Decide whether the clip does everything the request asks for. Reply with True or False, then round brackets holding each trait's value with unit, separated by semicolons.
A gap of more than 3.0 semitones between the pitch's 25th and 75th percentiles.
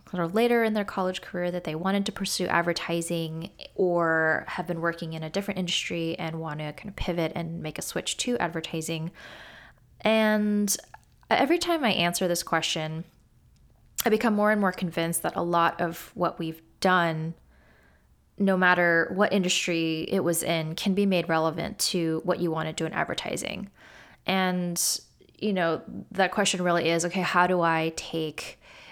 False (2.7 semitones)